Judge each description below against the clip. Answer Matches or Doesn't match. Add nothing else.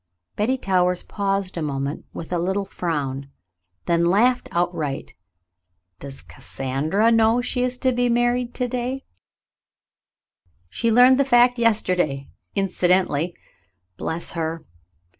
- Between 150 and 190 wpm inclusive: Doesn't match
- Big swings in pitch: Matches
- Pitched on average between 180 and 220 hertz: Matches